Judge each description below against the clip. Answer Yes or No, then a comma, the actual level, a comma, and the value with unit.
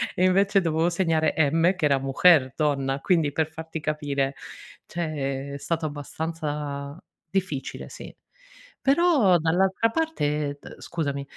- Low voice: No, medium, 160 Hz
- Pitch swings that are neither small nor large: Yes, average, 3.8 semitones